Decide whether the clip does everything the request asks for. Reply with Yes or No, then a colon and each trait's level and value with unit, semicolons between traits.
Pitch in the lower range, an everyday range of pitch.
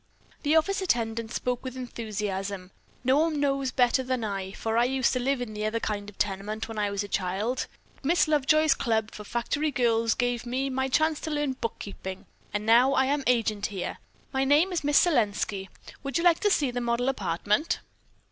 No: high, 245 Hz; average, 4.5 semitones